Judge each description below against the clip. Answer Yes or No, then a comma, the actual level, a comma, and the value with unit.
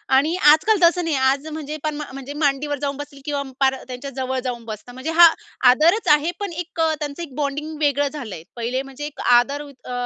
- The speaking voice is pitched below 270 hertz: No, very high, 285 Hz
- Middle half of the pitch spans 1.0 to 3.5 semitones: Yes, average, 2.8 semitones